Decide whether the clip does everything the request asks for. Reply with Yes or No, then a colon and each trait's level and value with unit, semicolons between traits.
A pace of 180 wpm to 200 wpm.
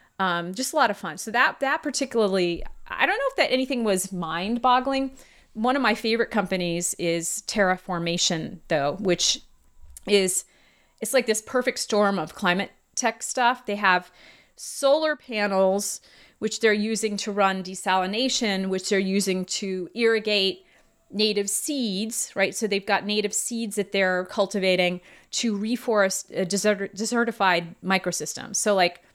No: average, 145 wpm